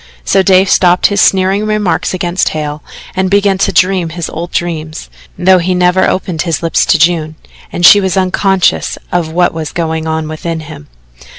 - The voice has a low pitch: No, medium, 175 Hz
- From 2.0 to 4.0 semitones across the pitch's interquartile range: Yes, average, 2.7 semitones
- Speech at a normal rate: Yes, average, 180 wpm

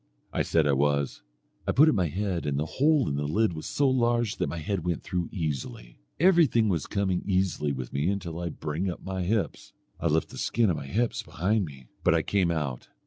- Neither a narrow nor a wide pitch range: No, wide, 5.9 semitones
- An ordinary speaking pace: No, fast, 235 wpm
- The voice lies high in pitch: No, very low, 90 Hz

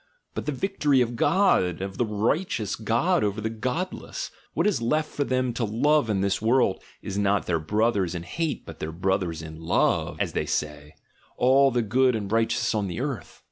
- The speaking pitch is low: Yes, low, 110 Hz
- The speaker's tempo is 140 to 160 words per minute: No, average, 195 wpm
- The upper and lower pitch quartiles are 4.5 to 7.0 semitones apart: Yes, average, 5.3 semitones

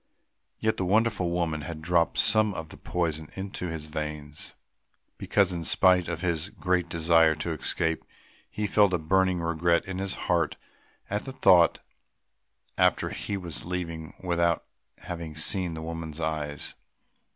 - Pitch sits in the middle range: No, very low, 85 Hz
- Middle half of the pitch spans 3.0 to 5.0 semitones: No, narrow, 2.5 semitones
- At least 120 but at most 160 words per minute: Yes, average, 150 wpm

